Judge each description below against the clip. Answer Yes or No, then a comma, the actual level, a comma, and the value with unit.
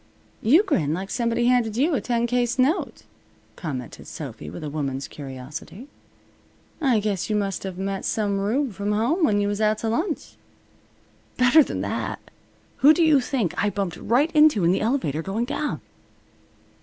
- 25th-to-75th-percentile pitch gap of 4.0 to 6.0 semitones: Yes, average, 5.2 semitones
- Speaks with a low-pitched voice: No, high, 215 Hz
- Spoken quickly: No, average, 170 wpm